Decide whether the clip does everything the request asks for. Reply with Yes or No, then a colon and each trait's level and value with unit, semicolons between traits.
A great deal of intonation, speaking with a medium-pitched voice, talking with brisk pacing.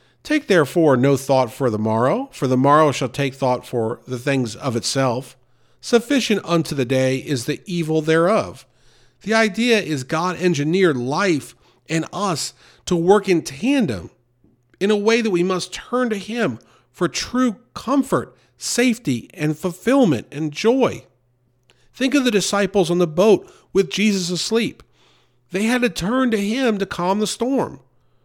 No: wide, 8.6 semitones; medium, 175 Hz; average, 160 wpm